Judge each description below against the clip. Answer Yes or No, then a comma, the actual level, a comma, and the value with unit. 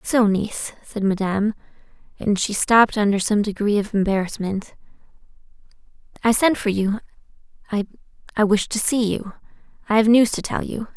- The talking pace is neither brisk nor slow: No, slow, 130 wpm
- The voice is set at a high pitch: Yes, high, 210 Hz